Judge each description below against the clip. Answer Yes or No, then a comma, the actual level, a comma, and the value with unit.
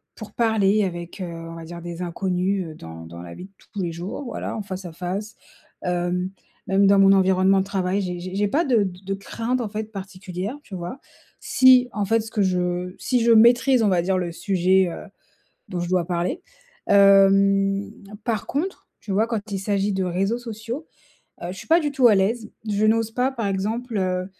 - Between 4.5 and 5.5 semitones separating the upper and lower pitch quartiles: No, average, 3.3 semitones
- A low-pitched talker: No, high, 195 Hz